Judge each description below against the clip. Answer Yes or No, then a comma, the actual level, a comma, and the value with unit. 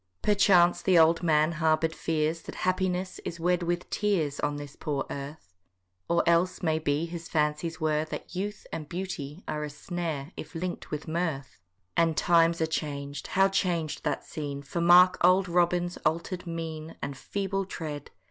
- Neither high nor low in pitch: Yes, medium, 165 Hz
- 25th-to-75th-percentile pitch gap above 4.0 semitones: No, average, 2.7 semitones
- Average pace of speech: Yes, average, 165 wpm